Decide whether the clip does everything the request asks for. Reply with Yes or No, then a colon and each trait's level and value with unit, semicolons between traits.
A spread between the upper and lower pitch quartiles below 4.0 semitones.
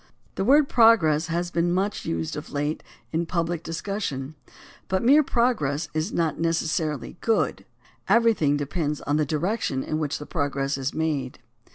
No: average, 4.5 semitones